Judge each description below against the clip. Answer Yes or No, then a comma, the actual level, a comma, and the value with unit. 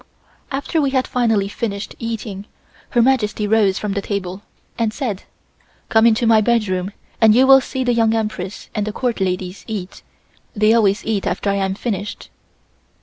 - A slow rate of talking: No, average, 170 wpm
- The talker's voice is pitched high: Yes, high, 215 Hz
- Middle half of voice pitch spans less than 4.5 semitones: Yes, average, 2.8 semitones